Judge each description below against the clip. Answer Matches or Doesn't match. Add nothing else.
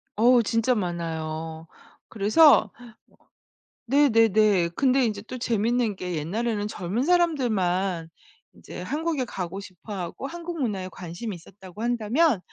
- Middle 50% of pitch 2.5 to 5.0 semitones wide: Doesn't match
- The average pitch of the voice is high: Matches